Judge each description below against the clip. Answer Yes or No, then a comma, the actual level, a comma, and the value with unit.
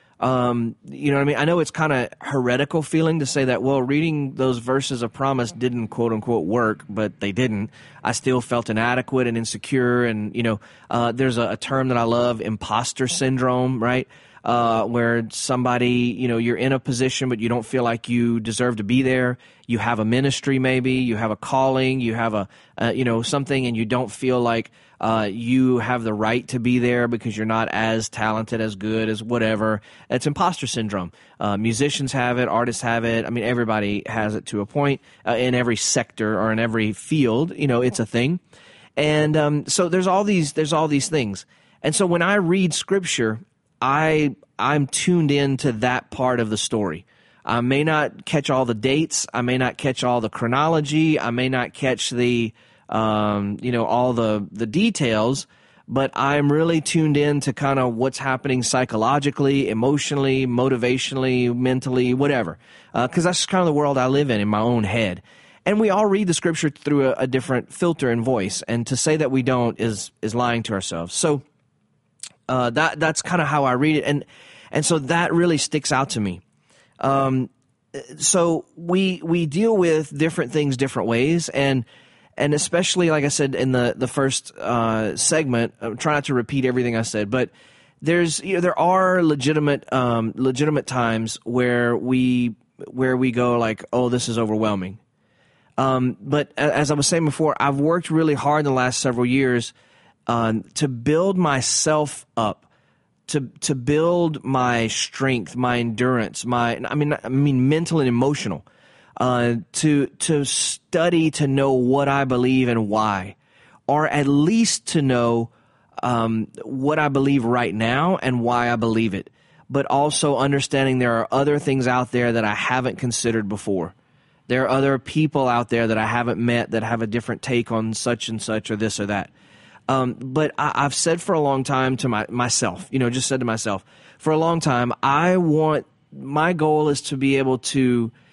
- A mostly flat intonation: No, average, 3.8 semitones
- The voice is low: Yes, low, 130 Hz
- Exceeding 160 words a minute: Yes, average, 200 wpm